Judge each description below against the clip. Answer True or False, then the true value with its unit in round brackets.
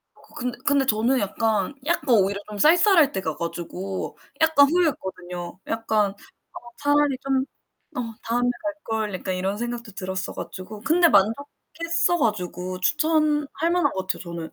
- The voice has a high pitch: True (230 Hz)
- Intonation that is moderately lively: False (7.5 semitones)